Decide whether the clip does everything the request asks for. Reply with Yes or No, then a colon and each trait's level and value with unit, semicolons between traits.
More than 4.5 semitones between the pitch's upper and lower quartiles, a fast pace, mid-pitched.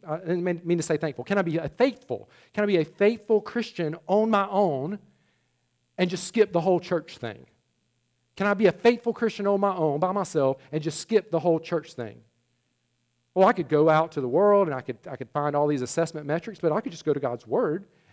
Yes: average, 5.3 semitones; fast, 230 wpm; medium, 170 Hz